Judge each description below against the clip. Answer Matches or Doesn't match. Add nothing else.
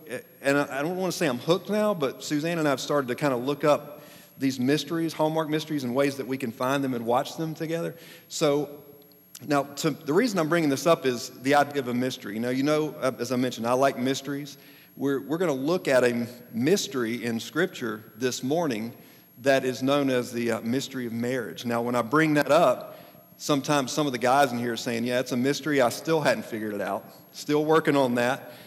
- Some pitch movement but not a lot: Matches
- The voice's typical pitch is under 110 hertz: Doesn't match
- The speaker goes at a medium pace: Doesn't match